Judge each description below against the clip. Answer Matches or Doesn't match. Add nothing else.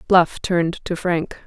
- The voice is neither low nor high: Matches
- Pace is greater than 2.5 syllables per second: Matches